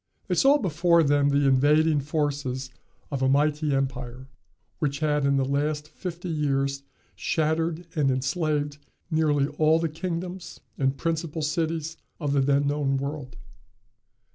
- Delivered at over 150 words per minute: No, average, 140 wpm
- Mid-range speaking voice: Yes, medium, 150 Hz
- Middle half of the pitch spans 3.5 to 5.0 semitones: No, narrow, 2.5 semitones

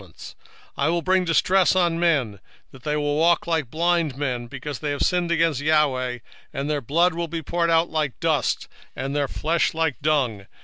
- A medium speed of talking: No, fast, 210 wpm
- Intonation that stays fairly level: No, average, 3.3 semitones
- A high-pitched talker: No, medium, 155 Hz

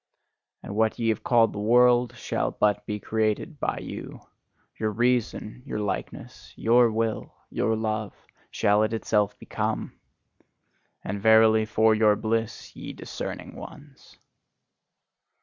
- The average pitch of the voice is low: Yes, low, 110 Hz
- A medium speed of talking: No, slow, 130 wpm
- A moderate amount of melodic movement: No, narrow, 1.5 semitones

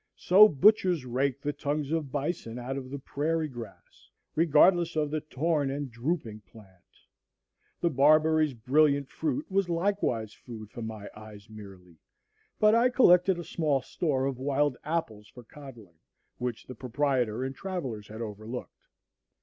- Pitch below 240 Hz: Yes, medium, 140 Hz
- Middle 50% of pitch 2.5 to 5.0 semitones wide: No, wide, 5.5 semitones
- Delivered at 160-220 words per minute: No, average, 150 wpm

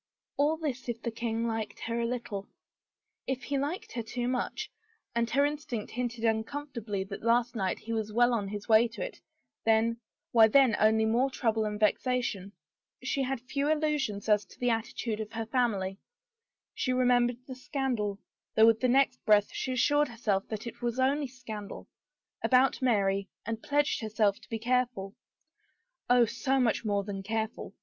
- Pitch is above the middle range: Yes, high, 235 Hz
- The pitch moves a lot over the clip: No, average, 2.9 semitones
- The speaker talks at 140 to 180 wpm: No, average, 190 wpm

